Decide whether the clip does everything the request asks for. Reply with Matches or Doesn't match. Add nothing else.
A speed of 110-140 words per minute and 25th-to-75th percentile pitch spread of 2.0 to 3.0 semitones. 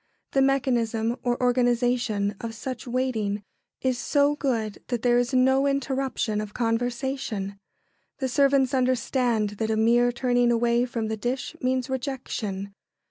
Matches